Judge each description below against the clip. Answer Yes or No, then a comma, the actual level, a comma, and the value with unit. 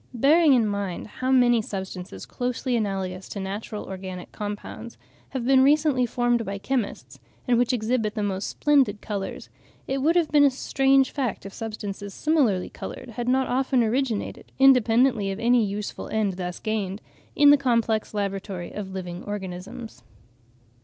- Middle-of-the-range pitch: No, high, 220 Hz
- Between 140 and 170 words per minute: Yes, average, 155 wpm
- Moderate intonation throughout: Yes, average, 4.6 semitones